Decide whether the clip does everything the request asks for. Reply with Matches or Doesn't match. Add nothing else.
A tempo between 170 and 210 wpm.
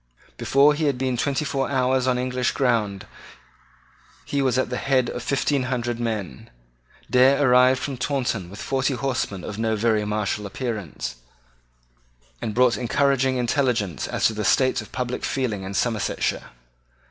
Doesn't match